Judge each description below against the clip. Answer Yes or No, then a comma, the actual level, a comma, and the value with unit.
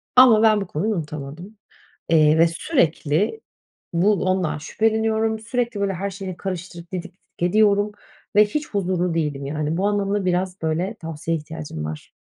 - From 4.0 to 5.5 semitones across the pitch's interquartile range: Yes, average, 4.6 semitones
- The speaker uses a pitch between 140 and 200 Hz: Yes, medium, 185 Hz